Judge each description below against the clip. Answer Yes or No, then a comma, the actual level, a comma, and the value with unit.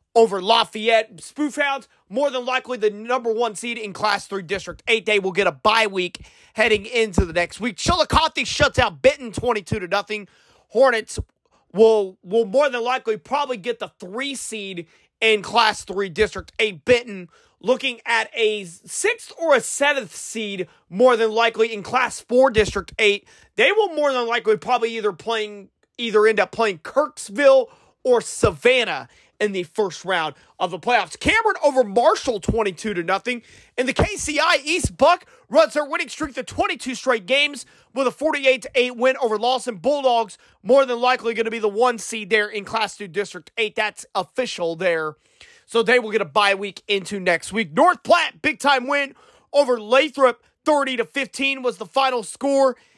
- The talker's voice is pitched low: No, high, 230 Hz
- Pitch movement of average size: Yes, average, 4.1 semitones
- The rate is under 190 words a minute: Yes, average, 180 wpm